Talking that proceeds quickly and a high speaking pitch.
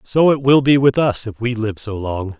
No: fast, 275 wpm; low, 120 Hz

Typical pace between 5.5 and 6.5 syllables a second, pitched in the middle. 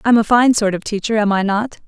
No: 5.9 syllables/s; high, 215 Hz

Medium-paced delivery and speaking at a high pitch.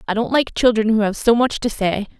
No: fast, 275 wpm; high, 225 Hz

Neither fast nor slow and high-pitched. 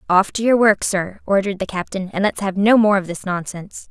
No: fast, 245 wpm; high, 195 Hz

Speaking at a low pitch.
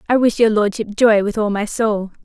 No: high, 215 Hz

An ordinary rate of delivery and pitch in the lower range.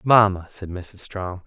Yes: average, 165 wpm; very low, 95 Hz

